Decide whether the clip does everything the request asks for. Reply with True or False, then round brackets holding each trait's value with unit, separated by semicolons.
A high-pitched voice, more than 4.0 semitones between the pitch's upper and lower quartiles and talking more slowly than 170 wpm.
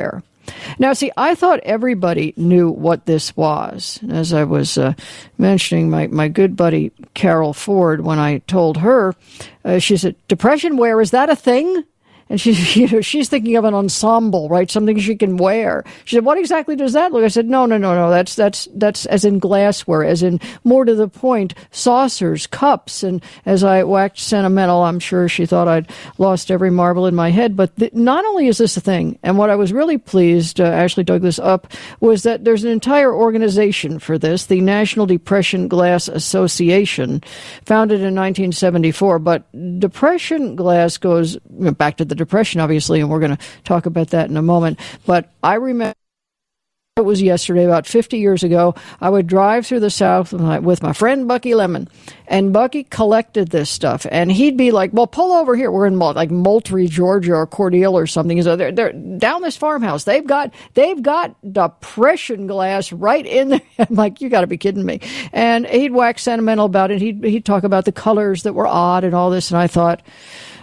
False (195 Hz; 4.7 semitones; 205 wpm)